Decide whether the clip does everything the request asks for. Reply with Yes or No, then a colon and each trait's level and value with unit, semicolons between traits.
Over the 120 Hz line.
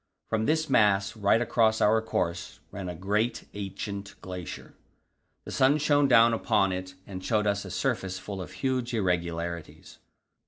No: low, 100 Hz